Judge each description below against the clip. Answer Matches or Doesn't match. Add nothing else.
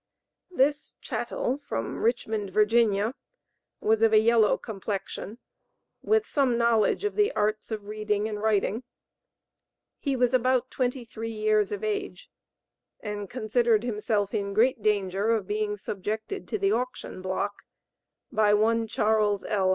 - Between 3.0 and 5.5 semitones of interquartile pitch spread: Doesn't match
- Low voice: Doesn't match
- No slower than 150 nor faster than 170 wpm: Doesn't match